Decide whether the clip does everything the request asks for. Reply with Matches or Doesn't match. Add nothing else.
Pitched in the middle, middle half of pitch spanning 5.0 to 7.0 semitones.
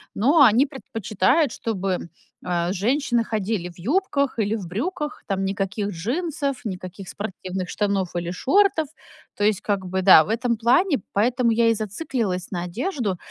Doesn't match